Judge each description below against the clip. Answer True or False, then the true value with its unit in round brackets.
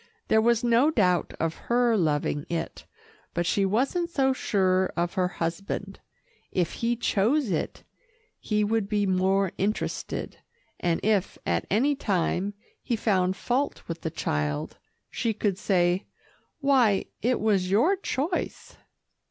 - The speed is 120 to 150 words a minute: True (135 wpm)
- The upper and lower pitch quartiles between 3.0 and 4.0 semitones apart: False (4.6 semitones)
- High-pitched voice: True (200 Hz)